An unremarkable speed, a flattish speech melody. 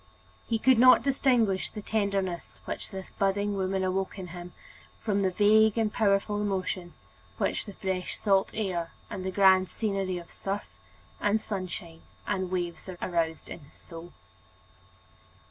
Yes: average, 145 wpm; narrow, 2.2 semitones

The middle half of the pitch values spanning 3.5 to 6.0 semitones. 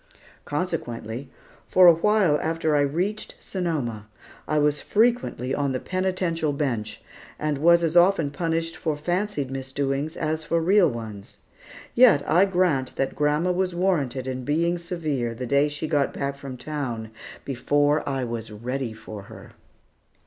Yes: average, 4.5 semitones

